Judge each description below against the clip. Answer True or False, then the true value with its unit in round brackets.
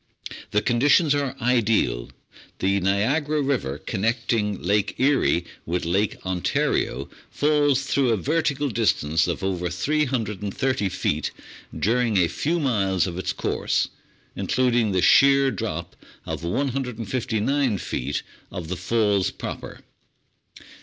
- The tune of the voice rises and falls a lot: True (6.3 semitones)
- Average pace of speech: False (115 wpm)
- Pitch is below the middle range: True (115 Hz)